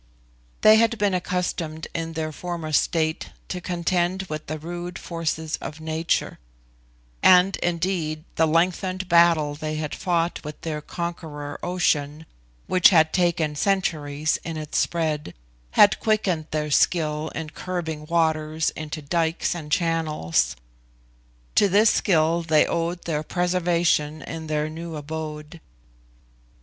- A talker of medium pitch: Yes, medium, 165 Hz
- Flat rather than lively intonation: Yes, narrow, 2.3 semitones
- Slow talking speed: Yes, slow, 130 wpm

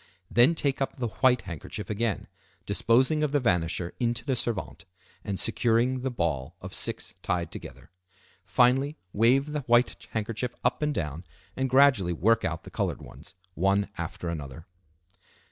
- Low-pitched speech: Yes, low, 115 Hz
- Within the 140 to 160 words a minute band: Yes, average, 155 wpm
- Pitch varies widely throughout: Yes, wide, 6.6 semitones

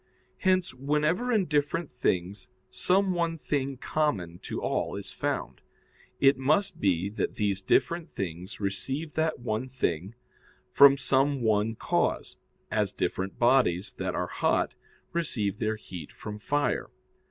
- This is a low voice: Yes, low, 130 Hz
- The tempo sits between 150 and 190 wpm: No, slow, 135 wpm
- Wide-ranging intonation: Yes, wide, 7.0 semitones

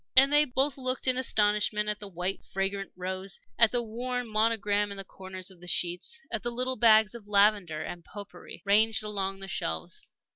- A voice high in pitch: Yes, high, 210 Hz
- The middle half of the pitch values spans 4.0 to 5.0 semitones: No, average, 3.5 semitones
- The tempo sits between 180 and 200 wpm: Yes, average, 195 wpm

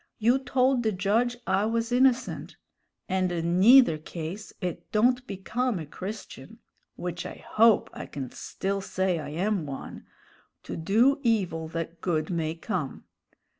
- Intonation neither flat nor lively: No, wide, 5.7 semitones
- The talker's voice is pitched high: Yes, high, 195 Hz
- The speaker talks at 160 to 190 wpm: No, average, 145 wpm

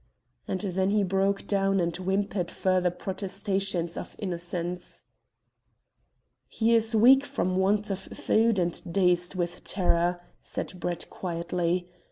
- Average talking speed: No, slow, 125 wpm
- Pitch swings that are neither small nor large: No, narrow, 2.2 semitones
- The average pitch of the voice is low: No, medium, 185 Hz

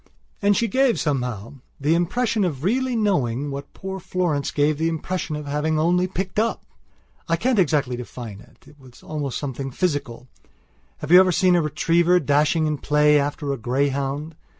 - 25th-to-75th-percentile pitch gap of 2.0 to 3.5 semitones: No, average, 4.5 semitones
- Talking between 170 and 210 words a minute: Yes, average, 175 wpm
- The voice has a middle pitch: Yes, medium, 150 Hz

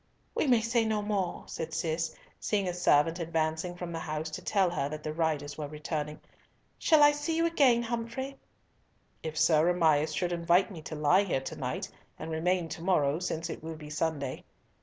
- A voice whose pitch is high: No, medium, 165 Hz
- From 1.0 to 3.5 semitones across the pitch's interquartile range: No, average, 4.3 semitones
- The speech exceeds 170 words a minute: Yes, average, 195 wpm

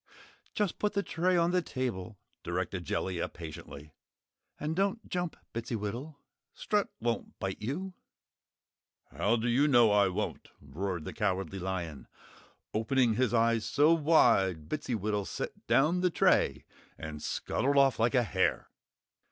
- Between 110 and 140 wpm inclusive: Yes, slow, 135 wpm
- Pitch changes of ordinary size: No, wide, 8.1 semitones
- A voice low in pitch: Yes, low, 115 Hz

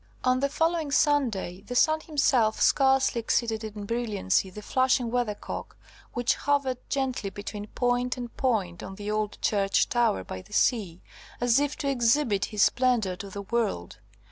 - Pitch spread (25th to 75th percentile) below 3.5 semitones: No, average, 4.2 semitones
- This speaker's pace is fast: No, average, 160 wpm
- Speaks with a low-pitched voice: No, high, 235 Hz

